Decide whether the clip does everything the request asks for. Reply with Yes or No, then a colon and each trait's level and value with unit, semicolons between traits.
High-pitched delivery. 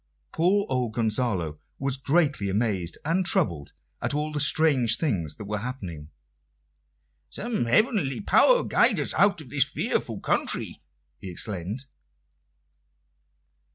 No: low, 125 Hz